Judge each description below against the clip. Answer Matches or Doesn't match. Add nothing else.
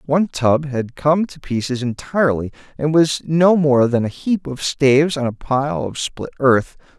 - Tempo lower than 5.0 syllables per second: Matches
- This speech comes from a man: Matches